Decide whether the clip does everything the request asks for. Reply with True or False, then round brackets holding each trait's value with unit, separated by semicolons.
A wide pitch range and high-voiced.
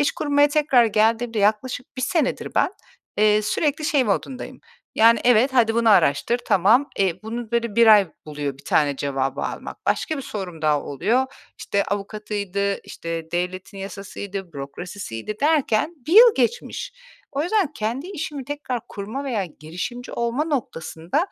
True (6.0 semitones; 220 Hz)